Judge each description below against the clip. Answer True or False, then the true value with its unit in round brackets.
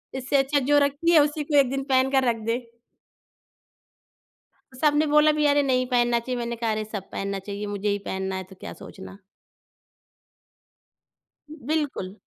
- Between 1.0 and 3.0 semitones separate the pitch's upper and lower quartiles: False (5.1 semitones)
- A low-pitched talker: False (260 Hz)